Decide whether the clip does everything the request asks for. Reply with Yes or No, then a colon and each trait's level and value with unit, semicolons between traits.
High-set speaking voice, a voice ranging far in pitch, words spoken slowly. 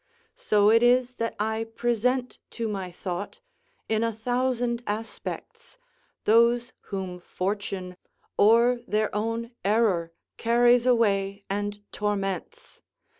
No: high, 225 Hz; average, 3.0 semitones; slow, 110 wpm